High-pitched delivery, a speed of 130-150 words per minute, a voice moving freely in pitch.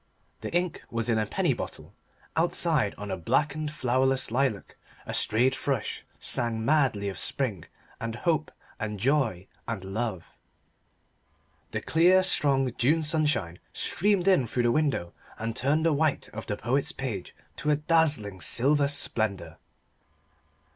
No: low, 130 Hz; average, 140 wpm; wide, 5.8 semitones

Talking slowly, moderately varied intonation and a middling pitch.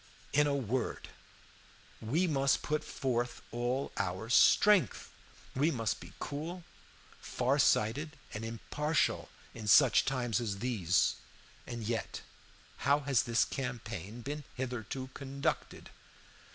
No: slow, 115 wpm; average, 3.9 semitones; low, 125 Hz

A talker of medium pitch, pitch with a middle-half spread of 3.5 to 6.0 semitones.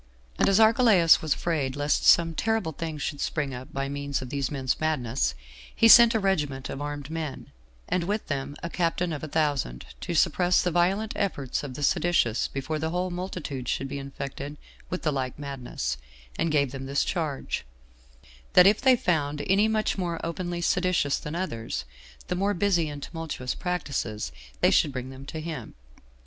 Yes: medium, 155 Hz; average, 4.5 semitones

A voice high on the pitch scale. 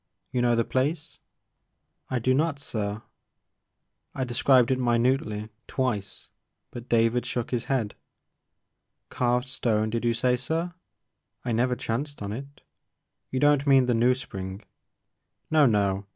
No: low, 125 Hz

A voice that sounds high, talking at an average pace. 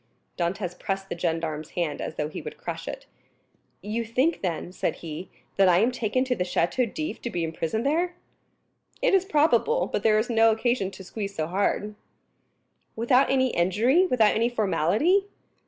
Yes: high, 215 Hz; average, 175 wpm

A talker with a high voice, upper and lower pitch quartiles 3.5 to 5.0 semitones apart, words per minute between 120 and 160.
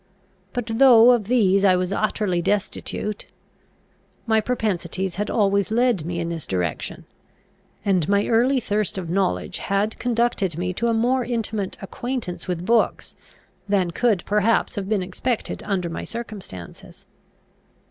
Yes: high, 205 Hz; average, 4.0 semitones; average, 140 wpm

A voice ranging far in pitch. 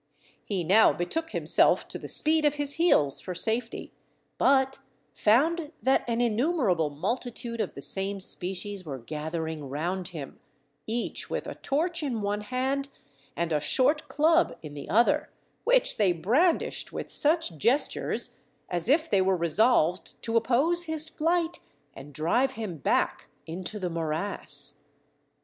Yes: wide, 8.9 semitones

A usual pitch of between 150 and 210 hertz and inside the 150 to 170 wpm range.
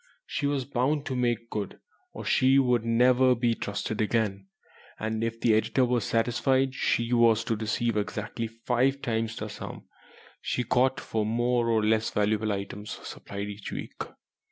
No: low, 115 Hz; average, 160 wpm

